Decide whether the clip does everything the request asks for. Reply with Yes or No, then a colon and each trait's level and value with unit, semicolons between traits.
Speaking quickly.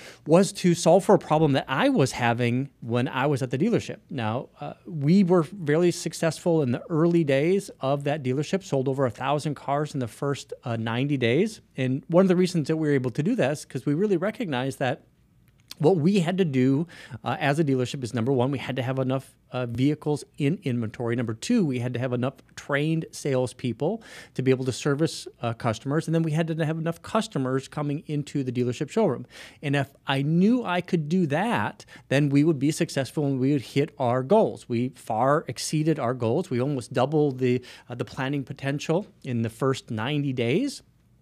Yes: fast, 210 wpm